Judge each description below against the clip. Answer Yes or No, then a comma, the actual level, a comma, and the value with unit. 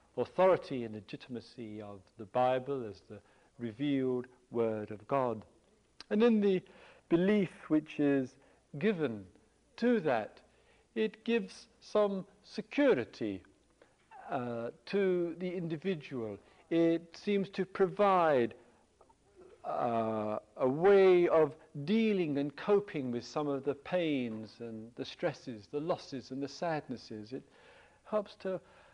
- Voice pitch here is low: No, medium, 150 Hz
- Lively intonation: Yes, wide, 8.2 semitones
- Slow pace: Yes, slow, 115 wpm